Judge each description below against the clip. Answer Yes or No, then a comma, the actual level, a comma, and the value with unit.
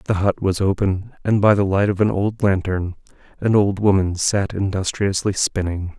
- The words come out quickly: No, average, 180 wpm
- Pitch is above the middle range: No, low, 100 Hz